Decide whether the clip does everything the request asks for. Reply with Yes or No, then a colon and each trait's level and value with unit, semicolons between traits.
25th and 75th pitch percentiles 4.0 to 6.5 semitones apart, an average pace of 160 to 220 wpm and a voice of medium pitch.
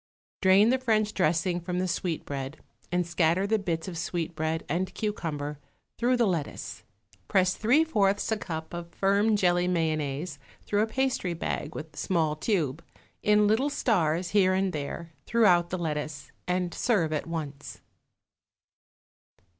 No: average, 4.3 semitones; average, 145 wpm; medium, 180 Hz